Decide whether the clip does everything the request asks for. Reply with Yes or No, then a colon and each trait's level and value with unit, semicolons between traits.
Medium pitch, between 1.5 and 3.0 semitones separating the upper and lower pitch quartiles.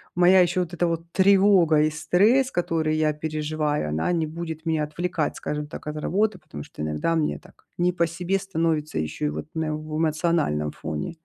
Yes: medium, 160 Hz; narrow, 2.6 semitones